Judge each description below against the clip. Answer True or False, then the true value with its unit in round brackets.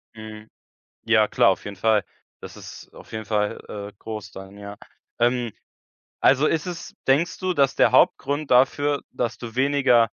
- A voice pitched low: True (120 Hz)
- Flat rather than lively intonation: False (4.6 semitones)